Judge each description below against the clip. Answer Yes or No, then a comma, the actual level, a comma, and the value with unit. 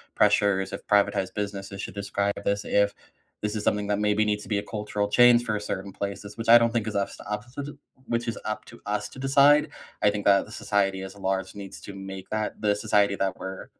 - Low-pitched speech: Yes, low, 105 Hz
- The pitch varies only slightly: Yes, narrow, 1.3 semitones